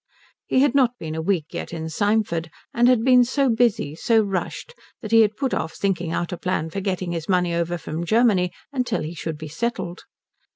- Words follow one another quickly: Yes, fast, 210 wpm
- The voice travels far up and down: Yes, wide, 5.8 semitones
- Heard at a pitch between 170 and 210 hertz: Yes, high, 190 Hz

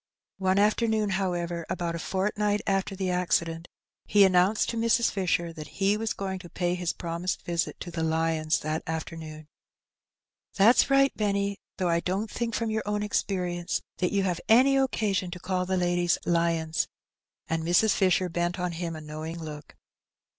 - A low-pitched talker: No, medium, 180 Hz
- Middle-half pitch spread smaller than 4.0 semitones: Yes, average, 3.2 semitones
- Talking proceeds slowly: No, average, 175 wpm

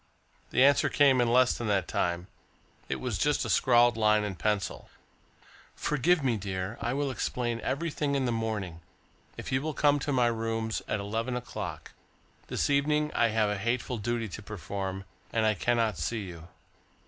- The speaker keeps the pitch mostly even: No, average, 3.9 semitones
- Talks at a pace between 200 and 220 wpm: No, average, 175 wpm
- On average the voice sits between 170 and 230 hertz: No, low, 115 Hz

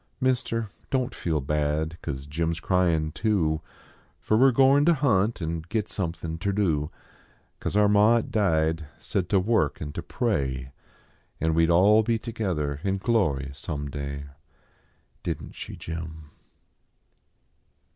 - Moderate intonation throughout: No, wide, 5.7 semitones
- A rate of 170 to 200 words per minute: No, average, 155 wpm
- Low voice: Yes, very low, 85 Hz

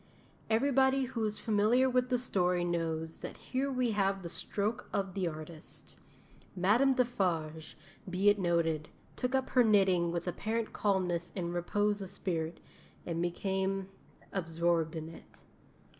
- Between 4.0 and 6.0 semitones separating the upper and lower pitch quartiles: Yes, average, 4.7 semitones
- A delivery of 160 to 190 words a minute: No, average, 145 wpm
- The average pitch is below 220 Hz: Yes, high, 190 Hz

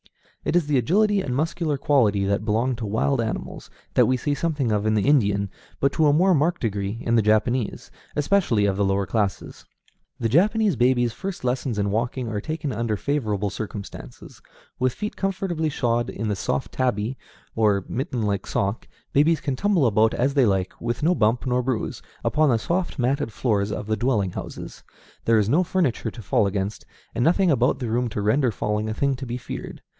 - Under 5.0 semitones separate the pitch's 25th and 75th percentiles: No, average, 5.3 semitones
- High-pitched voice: No, low, 120 Hz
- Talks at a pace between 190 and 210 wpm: Yes, average, 200 wpm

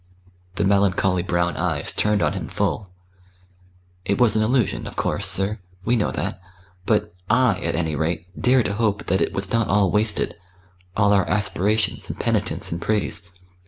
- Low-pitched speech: Yes, low, 100 Hz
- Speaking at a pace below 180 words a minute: Yes, average, 170 wpm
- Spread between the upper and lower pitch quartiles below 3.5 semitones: Yes, average, 2.9 semitones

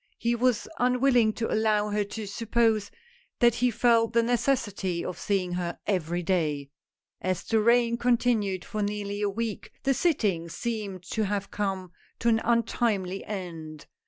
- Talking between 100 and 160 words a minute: Yes, average, 155 wpm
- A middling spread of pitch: Yes, average, 3.9 semitones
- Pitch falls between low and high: No, high, 210 Hz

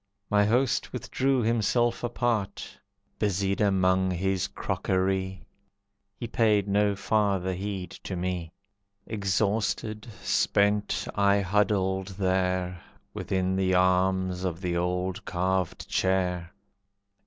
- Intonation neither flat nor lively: No, narrow, 2.0 semitones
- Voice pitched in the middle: No, very low, 95 Hz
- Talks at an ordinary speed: No, slow, 100 wpm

